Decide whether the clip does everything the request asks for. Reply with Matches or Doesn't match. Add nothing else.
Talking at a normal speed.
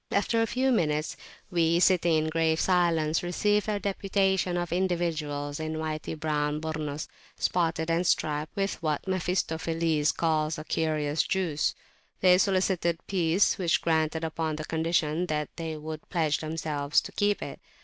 Matches